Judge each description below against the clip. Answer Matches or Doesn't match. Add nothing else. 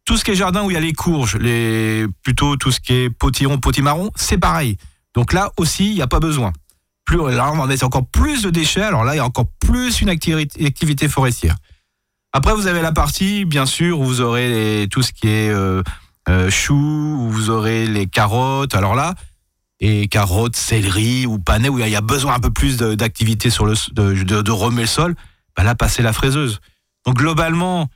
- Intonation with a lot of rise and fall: Matches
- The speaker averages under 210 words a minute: Doesn't match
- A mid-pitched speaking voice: Doesn't match